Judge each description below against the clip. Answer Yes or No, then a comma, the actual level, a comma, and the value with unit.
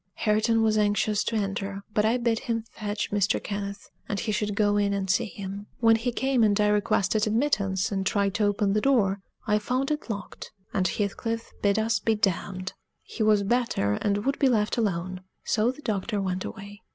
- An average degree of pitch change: No, narrow, 2.1 semitones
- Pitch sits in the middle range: No, high, 210 Hz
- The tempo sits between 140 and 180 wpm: No, average, 200 wpm